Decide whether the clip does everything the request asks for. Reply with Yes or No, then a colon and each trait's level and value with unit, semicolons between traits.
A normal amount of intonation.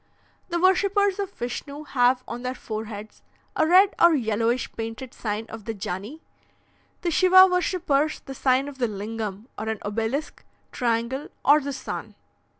No: wide, 6.0 semitones